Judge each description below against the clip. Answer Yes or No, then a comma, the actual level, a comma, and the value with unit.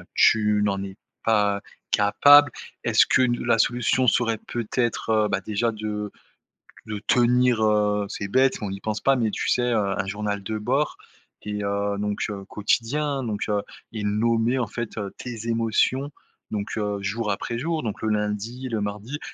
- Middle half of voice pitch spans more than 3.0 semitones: No, average, 2.7 semitones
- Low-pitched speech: Yes, low, 110 Hz